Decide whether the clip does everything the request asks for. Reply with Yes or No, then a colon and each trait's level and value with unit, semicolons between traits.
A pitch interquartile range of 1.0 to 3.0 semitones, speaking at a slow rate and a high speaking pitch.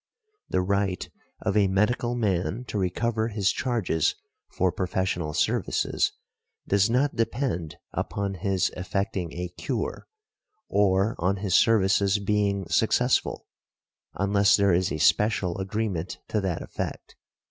No: narrow, 2.5 semitones; slow, 125 wpm; low, 100 Hz